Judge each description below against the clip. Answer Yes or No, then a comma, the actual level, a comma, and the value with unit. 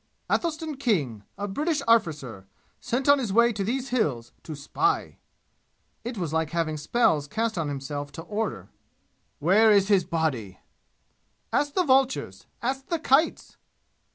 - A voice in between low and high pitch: No, high, 205 Hz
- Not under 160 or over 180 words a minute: No, average, 145 wpm